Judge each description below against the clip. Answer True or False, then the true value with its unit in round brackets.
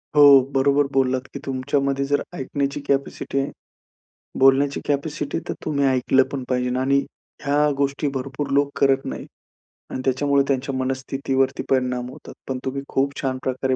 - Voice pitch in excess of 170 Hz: False (135 Hz)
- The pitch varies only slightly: True (1.2 semitones)